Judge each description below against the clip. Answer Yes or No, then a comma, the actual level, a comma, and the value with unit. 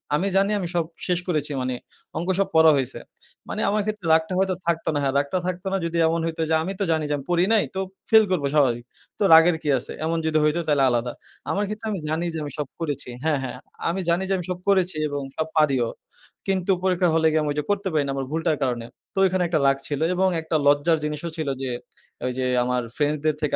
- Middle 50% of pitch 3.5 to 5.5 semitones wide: Yes, average, 4.0 semitones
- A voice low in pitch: No, medium, 160 Hz